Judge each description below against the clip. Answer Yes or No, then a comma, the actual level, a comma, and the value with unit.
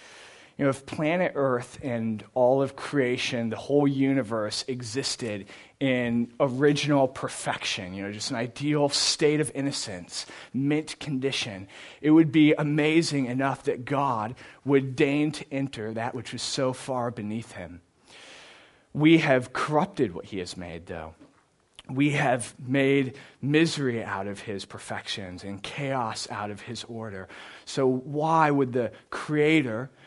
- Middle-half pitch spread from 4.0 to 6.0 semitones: Yes, average, 4.3 semitones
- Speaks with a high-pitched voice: No, low, 130 Hz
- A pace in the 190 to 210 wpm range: No, average, 140 wpm